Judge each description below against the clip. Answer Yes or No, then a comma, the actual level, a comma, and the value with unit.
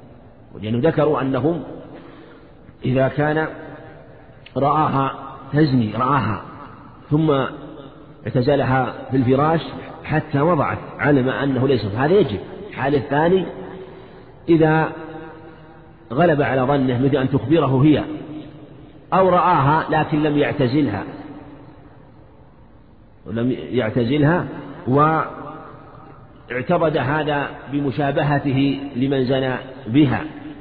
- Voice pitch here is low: No, medium, 145 Hz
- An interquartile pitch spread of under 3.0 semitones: Yes, narrow, 2.6 semitones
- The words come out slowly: No, average, 85 wpm